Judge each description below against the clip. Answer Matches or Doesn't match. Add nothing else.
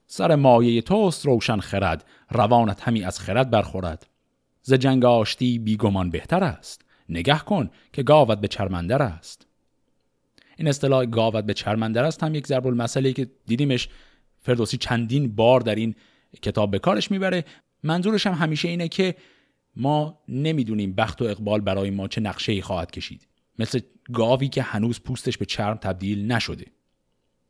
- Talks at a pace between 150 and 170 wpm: Matches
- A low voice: Matches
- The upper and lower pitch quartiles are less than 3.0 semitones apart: Doesn't match